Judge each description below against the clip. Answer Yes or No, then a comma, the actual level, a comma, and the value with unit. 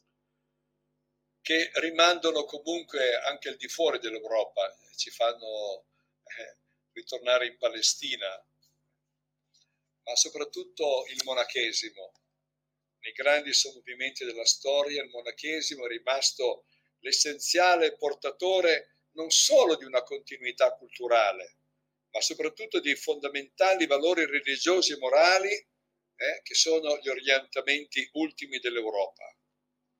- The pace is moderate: No, slow, 100 wpm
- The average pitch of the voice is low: No, medium, 160 Hz